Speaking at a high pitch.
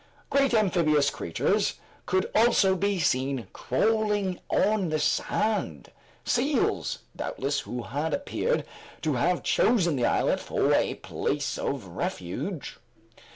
No: medium, 175 Hz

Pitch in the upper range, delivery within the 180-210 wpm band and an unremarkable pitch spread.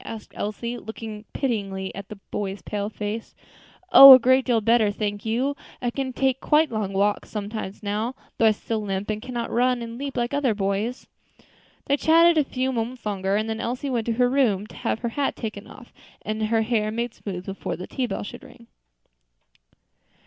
Yes: high, 225 Hz; average, 195 wpm; average, 3.3 semitones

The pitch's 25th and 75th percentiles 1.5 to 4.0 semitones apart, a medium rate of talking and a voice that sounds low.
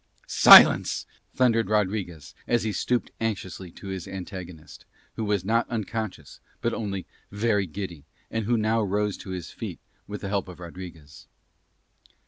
Yes: average, 3.3 semitones; average, 145 wpm; low, 100 Hz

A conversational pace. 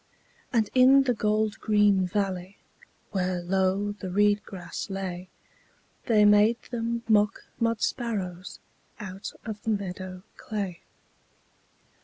No: slow, 115 wpm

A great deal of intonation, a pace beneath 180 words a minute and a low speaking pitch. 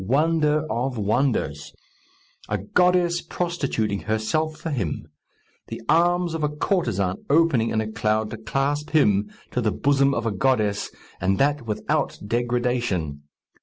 Yes: wide, 6.1 semitones; slow, 135 wpm; low, 125 Hz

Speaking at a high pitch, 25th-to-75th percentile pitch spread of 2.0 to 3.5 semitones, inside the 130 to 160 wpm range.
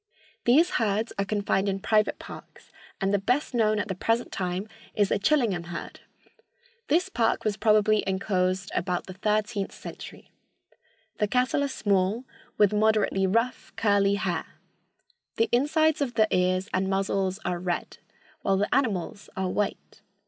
Yes: high, 205 Hz; average, 2.9 semitones; average, 150 wpm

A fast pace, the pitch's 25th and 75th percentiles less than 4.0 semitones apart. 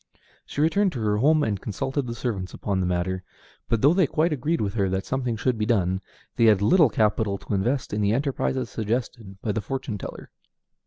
No: fast, 210 wpm; average, 4.9 semitones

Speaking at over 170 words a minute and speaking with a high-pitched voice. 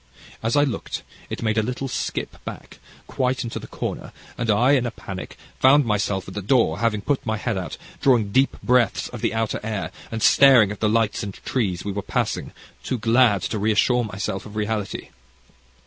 No: average, 195 wpm; low, 110 Hz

